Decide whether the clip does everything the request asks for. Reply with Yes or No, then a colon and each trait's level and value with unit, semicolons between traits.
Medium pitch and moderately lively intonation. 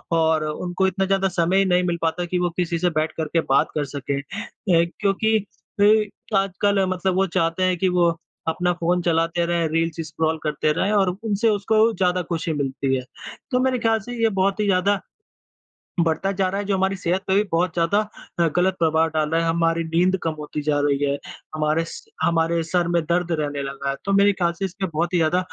Yes: medium, 175 Hz; average, 3.0 semitones